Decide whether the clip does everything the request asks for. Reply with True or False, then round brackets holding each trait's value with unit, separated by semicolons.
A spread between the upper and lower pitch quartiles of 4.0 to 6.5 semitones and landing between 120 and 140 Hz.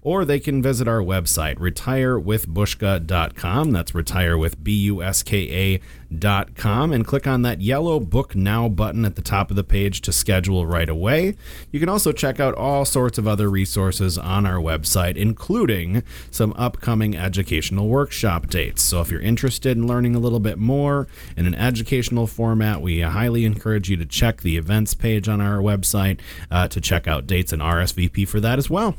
False (4.6 semitones; 105 Hz)